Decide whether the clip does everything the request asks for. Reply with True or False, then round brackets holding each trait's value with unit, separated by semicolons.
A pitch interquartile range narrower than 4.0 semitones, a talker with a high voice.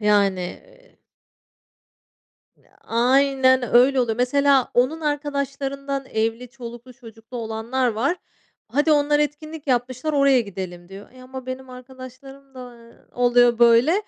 True (2.8 semitones; 255 Hz)